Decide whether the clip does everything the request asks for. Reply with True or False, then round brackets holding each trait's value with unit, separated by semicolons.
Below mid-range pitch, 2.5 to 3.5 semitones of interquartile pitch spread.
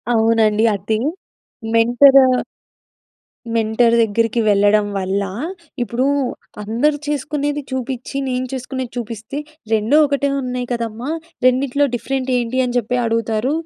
False (240 Hz; 2.9 semitones)